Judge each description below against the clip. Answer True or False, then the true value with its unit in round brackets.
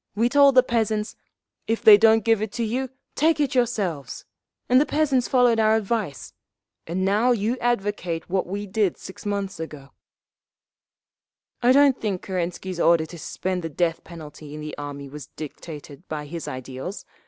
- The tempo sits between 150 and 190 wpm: True (165 wpm)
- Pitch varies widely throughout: True (6.3 semitones)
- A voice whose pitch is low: False (200 Hz)